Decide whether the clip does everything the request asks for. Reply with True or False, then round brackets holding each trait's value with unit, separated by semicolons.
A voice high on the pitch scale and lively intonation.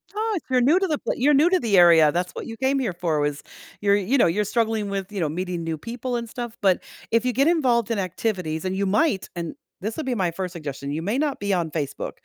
True (205 Hz; 6.2 semitones)